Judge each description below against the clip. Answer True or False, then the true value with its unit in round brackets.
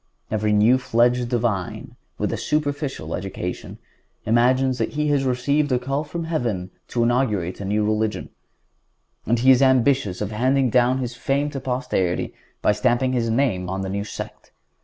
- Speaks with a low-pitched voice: True (120 Hz)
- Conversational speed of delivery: True (165 wpm)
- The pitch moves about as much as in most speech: True (3.9 semitones)